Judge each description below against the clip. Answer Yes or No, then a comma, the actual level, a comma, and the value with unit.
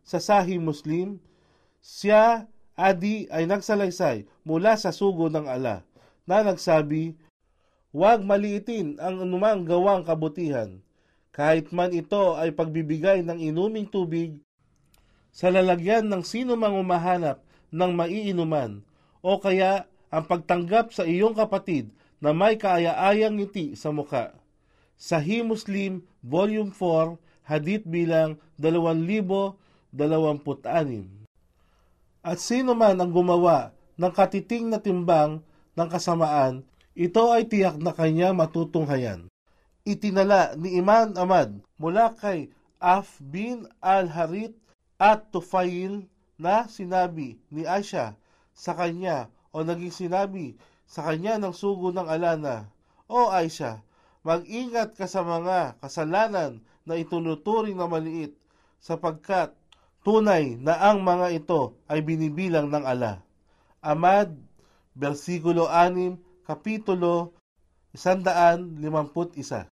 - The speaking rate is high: No, slow, 110 wpm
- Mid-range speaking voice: Yes, medium, 175 Hz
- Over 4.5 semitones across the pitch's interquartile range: No, average, 3.6 semitones